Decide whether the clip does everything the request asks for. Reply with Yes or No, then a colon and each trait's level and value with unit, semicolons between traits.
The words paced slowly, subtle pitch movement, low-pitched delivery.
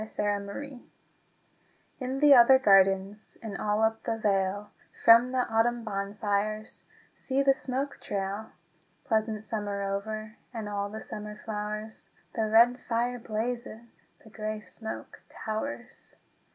No: slow, 130 wpm; narrow, 2.2 semitones; high, 220 Hz